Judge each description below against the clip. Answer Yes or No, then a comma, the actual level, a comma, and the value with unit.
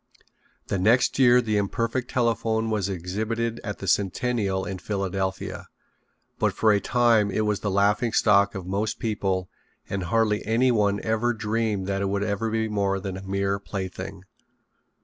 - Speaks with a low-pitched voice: Yes, low, 105 Hz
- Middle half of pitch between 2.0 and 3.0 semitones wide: Yes, narrow, 2.5 semitones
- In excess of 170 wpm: No, average, 160 wpm